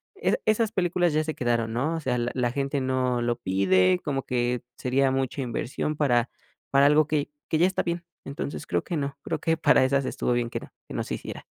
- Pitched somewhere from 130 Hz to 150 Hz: Yes, low, 135 Hz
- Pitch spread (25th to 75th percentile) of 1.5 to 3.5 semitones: No, average, 4.1 semitones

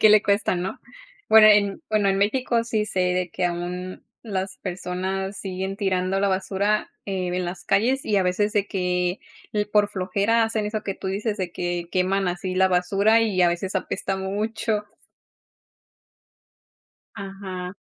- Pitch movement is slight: Yes, narrow, 2.2 semitones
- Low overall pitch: No, high, 195 Hz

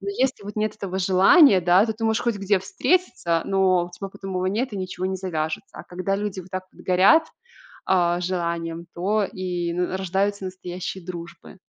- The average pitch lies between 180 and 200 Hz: Yes, high, 190 Hz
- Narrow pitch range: Yes, narrow, 2.3 semitones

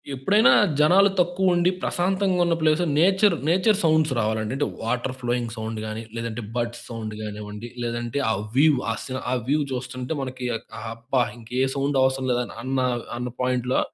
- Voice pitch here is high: No, low, 130 Hz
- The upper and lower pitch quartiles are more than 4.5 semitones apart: Yes, average, 5.3 semitones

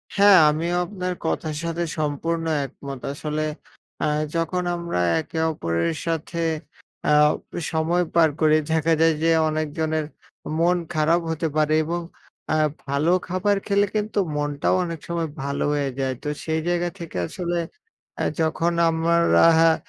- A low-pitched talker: No, medium, 165 Hz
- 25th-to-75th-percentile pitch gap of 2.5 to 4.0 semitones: No, narrow, 2.0 semitones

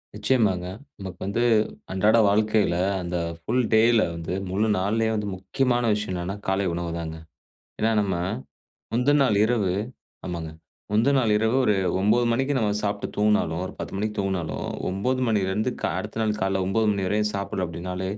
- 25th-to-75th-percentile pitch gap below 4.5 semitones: Yes, average, 3.0 semitones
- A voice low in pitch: Yes, low, 105 Hz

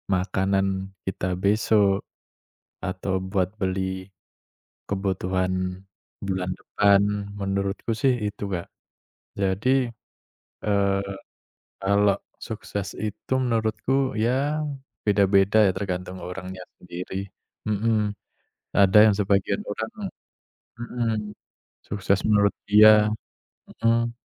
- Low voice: Yes, low, 100 Hz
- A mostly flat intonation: Yes, narrow, 2.2 semitones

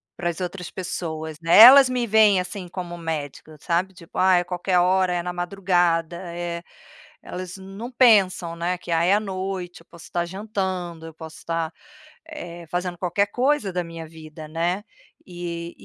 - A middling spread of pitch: No, narrow, 2.1 semitones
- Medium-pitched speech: Yes, medium, 175 Hz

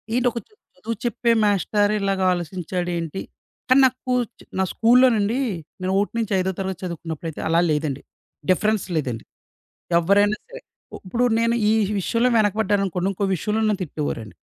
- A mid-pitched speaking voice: No, high, 200 Hz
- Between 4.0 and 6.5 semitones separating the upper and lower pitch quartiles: Yes, average, 4.6 semitones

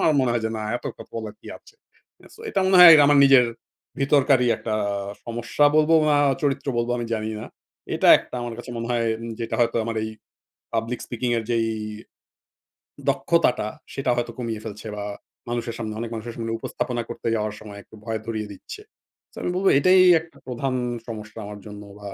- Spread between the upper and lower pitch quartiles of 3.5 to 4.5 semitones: No, average, 2.9 semitones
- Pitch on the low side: Yes, low, 115 Hz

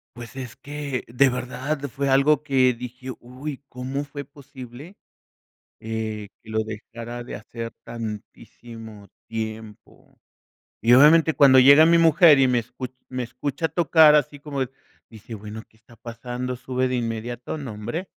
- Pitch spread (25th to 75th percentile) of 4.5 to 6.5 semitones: No, average, 3.6 semitones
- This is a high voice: No, low, 125 Hz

